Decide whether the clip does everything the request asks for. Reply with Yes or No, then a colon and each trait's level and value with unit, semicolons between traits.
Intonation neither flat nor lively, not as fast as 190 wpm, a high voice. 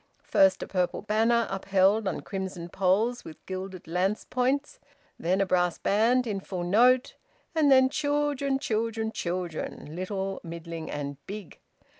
Yes: average, 4.6 semitones; average, 140 wpm; high, 195 Hz